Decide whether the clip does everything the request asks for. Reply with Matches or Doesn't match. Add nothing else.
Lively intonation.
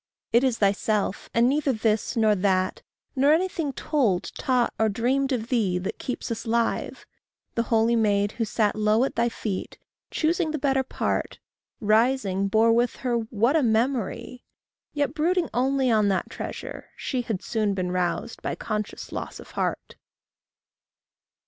Doesn't match